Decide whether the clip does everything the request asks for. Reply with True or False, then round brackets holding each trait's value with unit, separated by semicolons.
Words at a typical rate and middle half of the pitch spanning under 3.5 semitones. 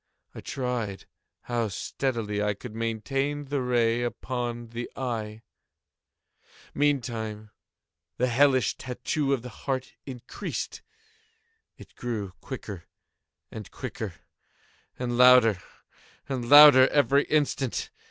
False (105 wpm; 2.9 semitones)